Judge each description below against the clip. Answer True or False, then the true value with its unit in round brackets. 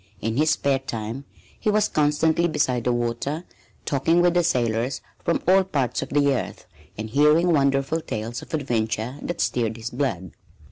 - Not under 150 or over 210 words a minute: True (170 wpm)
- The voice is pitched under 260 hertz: True (135 Hz)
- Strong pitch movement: False (4.9 semitones)